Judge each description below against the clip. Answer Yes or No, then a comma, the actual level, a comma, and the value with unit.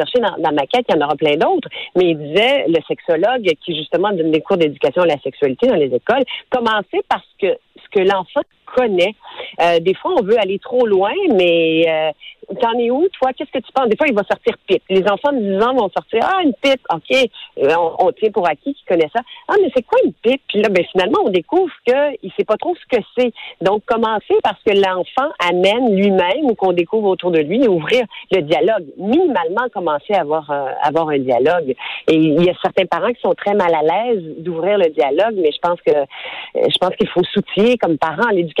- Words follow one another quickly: Yes, fast, 235 wpm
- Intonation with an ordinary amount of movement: No, wide, 7.8 semitones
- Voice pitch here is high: Yes, high, 210 Hz